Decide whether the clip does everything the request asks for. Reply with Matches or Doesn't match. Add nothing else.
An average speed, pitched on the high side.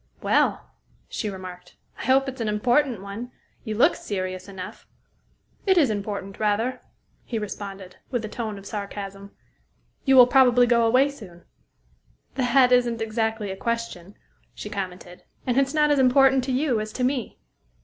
Matches